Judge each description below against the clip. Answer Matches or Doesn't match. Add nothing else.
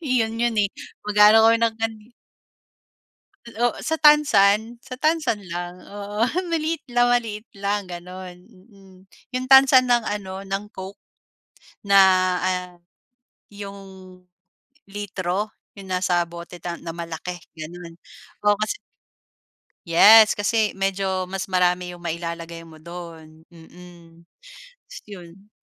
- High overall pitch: Matches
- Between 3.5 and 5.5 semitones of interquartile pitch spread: Matches